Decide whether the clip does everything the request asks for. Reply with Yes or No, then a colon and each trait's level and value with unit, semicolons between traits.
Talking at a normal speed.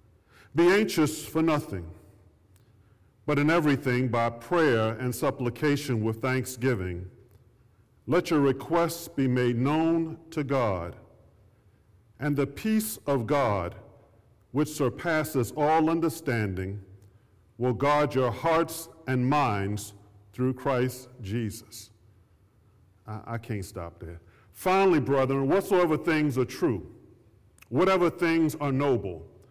No: slow, 110 wpm